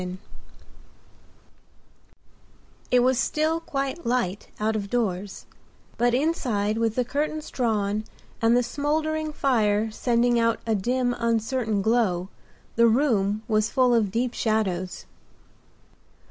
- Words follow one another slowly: Yes, slow, 120 wpm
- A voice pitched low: No, high, 230 Hz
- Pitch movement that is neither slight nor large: Yes, average, 3.3 semitones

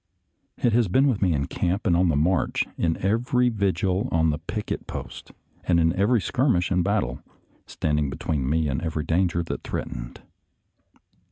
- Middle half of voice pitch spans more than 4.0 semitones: Yes, average, 4.6 semitones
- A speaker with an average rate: Yes, average, 170 wpm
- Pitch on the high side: No, very low, 90 Hz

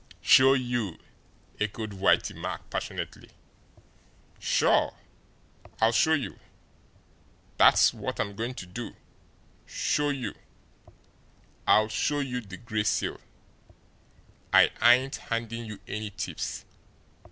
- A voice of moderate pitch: No, low, 115 Hz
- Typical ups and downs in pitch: Yes, average, 3.1 semitones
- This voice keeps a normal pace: No, slow, 105 wpm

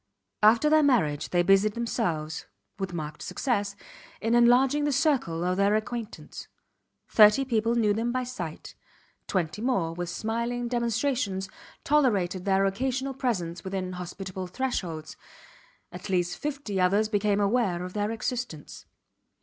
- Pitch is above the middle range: Yes, high, 210 Hz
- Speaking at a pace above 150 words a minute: No, slow, 135 wpm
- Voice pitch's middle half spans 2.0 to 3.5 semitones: No, average, 5.0 semitones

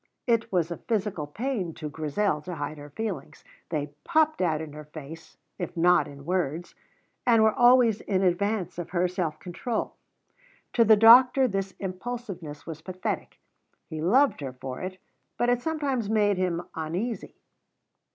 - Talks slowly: No, average, 160 wpm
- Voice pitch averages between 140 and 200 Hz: Yes, medium, 185 Hz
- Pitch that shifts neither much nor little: No, wide, 6.1 semitones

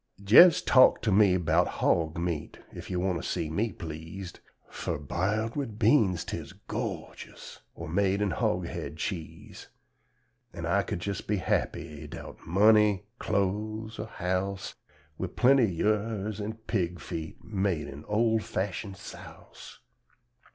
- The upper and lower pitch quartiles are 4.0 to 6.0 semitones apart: No, average, 3.6 semitones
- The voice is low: Yes, low, 100 Hz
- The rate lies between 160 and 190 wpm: No, average, 140 wpm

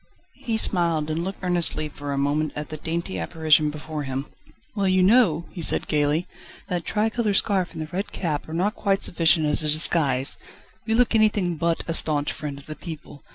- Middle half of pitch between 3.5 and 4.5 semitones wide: Yes, average, 3.8 semitones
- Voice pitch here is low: No, medium, 160 Hz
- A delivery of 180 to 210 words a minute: Yes, average, 200 wpm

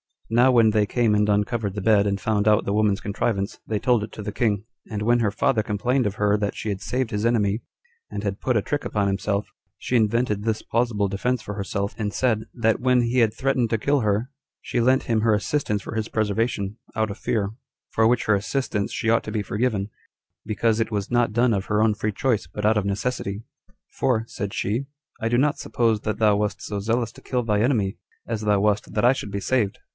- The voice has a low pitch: Yes, low, 110 Hz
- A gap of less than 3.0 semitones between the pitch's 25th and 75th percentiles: Yes, narrow, 2.4 semitones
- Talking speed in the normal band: No, fast, 230 wpm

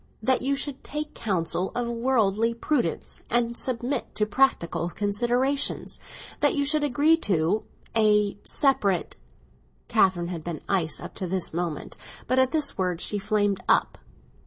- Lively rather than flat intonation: Yes, wide, 5.8 semitones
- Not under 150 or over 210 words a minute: No, slow, 135 wpm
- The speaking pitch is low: No, high, 220 Hz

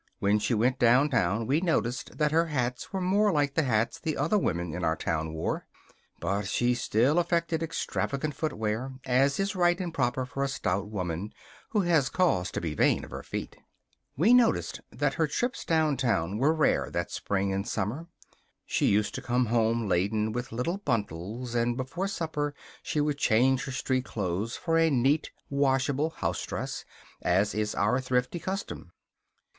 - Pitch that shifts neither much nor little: No, wide, 6.7 semitones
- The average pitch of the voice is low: Yes, low, 130 Hz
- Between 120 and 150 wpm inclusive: No, average, 170 wpm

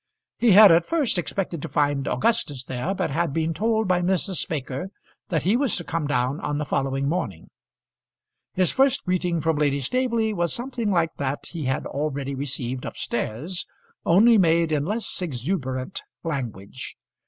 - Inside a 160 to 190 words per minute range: Yes, average, 165 wpm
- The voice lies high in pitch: No, medium, 165 Hz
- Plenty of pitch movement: Yes, wide, 5.7 semitones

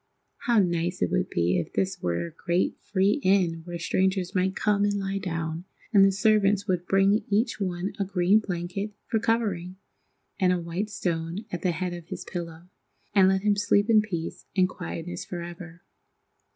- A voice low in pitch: No, medium, 185 Hz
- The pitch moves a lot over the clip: No, average, 2.8 semitones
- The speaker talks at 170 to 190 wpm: Yes, average, 180 wpm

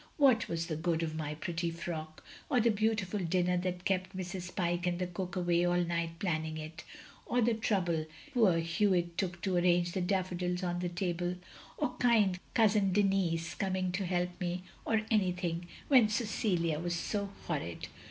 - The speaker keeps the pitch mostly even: Yes, narrow, 2.3 semitones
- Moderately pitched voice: Yes, medium, 180 Hz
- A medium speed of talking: Yes, average, 180 wpm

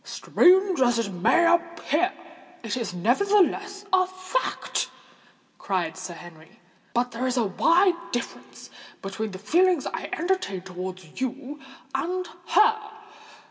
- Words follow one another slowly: Yes, slow, 125 wpm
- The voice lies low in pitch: No, very high, 275 Hz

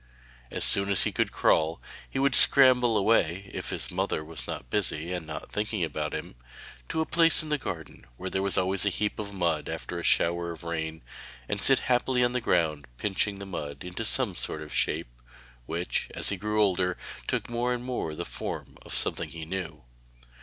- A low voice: Yes, very low, 95 Hz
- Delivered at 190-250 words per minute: Yes, average, 200 wpm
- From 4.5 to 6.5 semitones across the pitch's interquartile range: Yes, average, 5.2 semitones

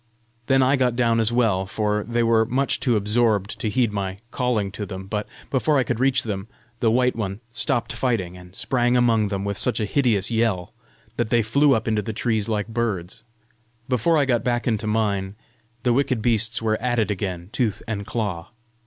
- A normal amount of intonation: Yes, average, 3.0 semitones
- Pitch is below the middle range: Yes, low, 115 Hz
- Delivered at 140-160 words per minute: No, average, 200 wpm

